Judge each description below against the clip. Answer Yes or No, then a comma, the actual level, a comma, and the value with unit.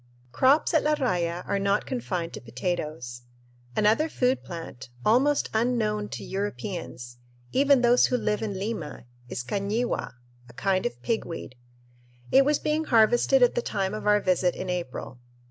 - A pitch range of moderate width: No, wide, 5.8 semitones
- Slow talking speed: No, average, 155 wpm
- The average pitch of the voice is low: No, high, 210 Hz